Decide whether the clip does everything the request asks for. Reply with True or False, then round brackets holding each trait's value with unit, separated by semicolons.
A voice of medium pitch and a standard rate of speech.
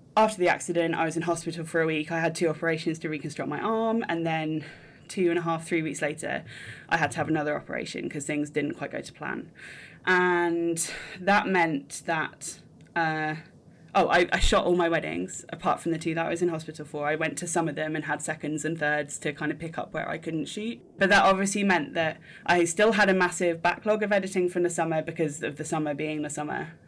False (165 Hz; 235 wpm)